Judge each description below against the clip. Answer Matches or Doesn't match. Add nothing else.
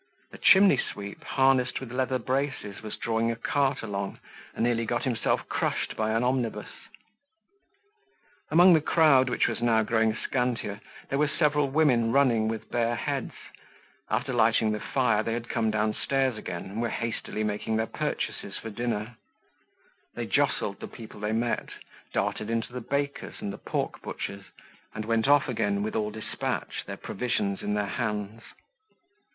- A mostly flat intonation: Doesn't match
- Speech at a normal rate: Matches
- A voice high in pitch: Doesn't match